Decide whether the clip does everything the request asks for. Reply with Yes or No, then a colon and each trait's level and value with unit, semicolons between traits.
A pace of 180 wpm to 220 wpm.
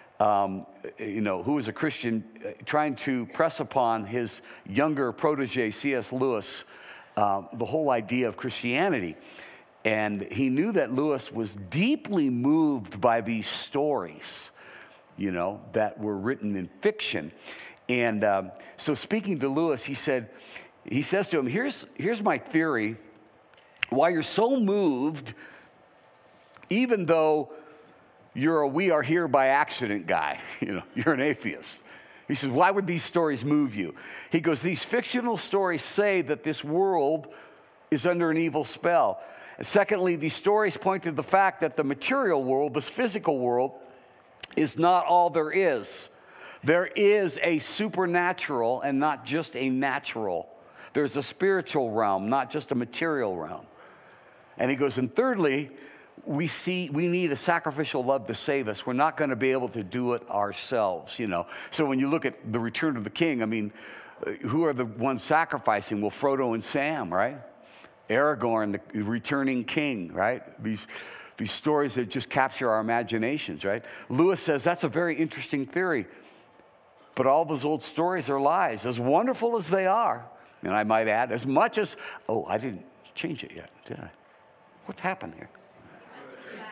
No: average, 165 wpm